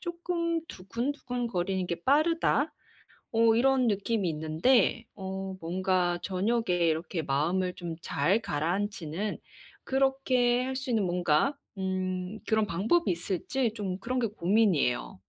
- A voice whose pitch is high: Yes, high, 200 Hz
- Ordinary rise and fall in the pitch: No, wide, 5.8 semitones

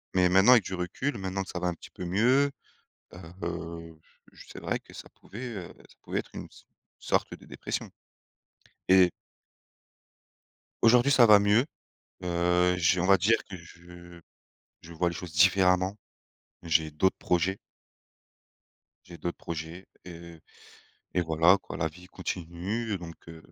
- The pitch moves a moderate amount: No, narrow, 2.3 semitones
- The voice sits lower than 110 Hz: Yes, very low, 90 Hz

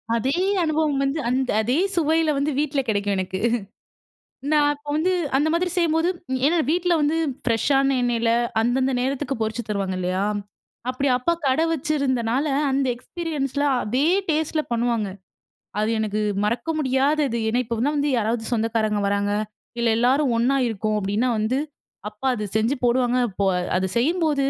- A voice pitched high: Yes, very high, 260 Hz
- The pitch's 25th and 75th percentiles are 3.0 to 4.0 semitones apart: No, average, 4.8 semitones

